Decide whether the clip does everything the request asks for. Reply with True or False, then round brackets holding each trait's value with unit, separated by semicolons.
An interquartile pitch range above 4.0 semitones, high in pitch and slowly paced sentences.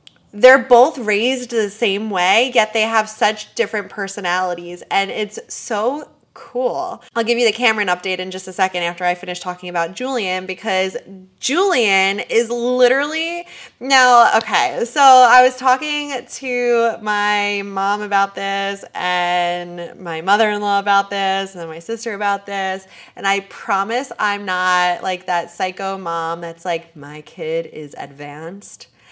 False (4.7 semitones; 200 Hz; 155 wpm)